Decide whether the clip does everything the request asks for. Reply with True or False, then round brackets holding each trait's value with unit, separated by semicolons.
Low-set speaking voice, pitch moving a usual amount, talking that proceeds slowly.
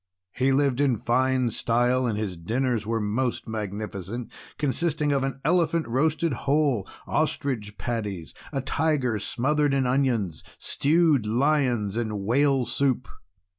True (125 Hz; 4.2 semitones; 130 wpm)